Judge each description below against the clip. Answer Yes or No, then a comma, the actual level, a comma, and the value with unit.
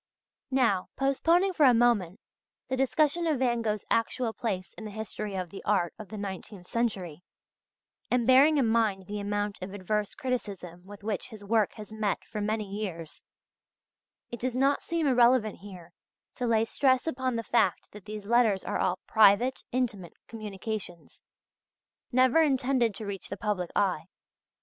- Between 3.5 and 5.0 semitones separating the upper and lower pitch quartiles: Yes, average, 4.0 semitones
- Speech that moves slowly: No, average, 165 wpm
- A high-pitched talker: Yes, high, 220 Hz